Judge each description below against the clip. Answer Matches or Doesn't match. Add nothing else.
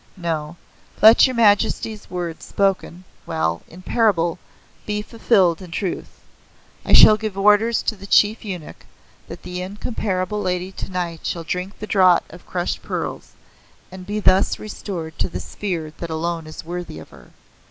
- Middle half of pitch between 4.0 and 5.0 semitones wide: Doesn't match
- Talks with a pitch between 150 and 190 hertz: Matches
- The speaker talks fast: Doesn't match